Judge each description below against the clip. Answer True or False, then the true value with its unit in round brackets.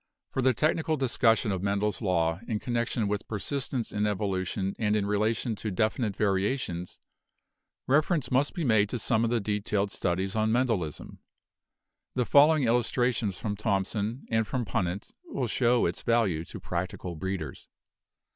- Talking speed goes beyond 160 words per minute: False (155 wpm)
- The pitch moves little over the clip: False (3.8 semitones)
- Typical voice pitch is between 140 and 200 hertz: False (110 Hz)